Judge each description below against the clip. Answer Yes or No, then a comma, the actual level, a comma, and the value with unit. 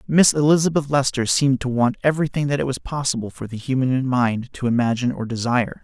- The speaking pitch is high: No, low, 130 Hz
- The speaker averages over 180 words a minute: Yes, average, 195 wpm